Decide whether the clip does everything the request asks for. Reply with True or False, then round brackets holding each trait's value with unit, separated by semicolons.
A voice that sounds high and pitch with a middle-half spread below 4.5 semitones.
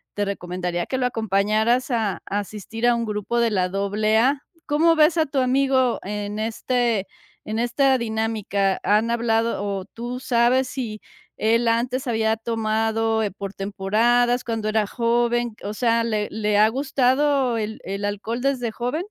True (225 Hz; 2.7 semitones)